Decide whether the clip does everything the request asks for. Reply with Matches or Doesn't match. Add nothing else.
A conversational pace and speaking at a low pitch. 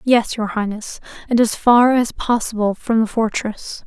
Doesn't match